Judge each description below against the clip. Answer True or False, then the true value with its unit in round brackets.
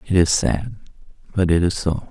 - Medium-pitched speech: False (90 Hz)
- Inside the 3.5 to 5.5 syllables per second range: True (4.9 syllables/s)